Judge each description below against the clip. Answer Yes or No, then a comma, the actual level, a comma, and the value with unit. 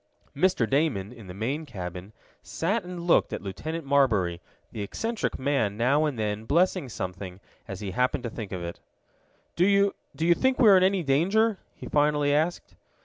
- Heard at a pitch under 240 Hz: Yes, medium, 140 Hz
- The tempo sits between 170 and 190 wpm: Yes, average, 185 wpm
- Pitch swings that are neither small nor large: No, wide, 8.8 semitones